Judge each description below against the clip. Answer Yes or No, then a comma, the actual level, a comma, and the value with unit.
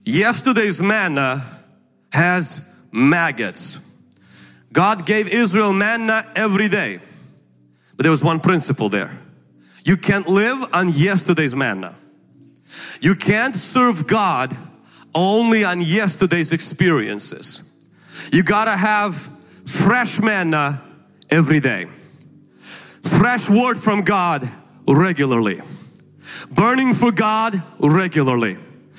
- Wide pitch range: Yes, wide, 6.1 semitones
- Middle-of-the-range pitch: Yes, medium, 180 Hz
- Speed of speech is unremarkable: No, slow, 95 wpm